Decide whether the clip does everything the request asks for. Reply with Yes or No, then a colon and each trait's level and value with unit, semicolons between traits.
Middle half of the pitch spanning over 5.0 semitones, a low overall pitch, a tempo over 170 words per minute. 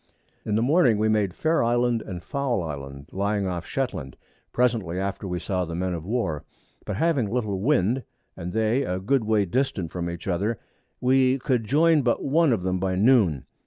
Yes: wide, 5.6 semitones; low, 105 Hz; average, 195 wpm